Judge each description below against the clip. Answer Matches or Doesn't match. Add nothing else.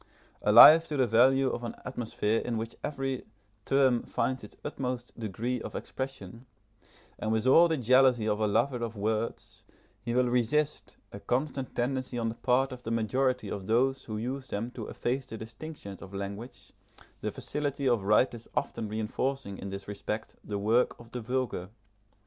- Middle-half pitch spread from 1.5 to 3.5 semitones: Matches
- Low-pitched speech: Matches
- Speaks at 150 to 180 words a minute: Matches